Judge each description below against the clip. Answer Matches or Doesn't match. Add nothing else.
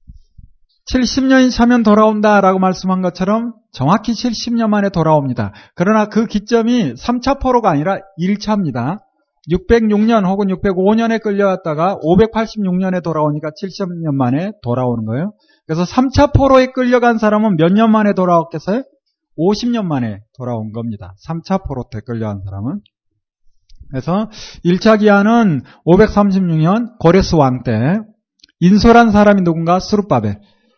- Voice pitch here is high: Matches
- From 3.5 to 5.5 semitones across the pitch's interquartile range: Doesn't match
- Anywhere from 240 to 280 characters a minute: Matches